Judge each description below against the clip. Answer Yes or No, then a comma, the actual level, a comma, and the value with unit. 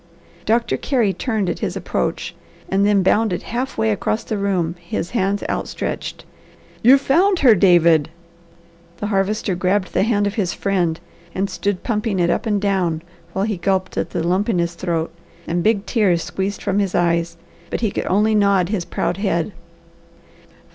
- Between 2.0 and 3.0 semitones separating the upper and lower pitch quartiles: No, average, 3.4 semitones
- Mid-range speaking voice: No, high, 195 Hz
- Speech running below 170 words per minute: No, average, 175 wpm